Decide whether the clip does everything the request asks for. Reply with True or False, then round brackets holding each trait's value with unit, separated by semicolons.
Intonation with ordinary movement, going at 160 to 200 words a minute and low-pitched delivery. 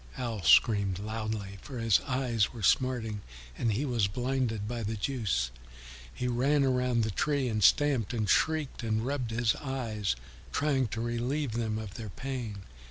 True (3.2 semitones; 165 wpm; 115 Hz)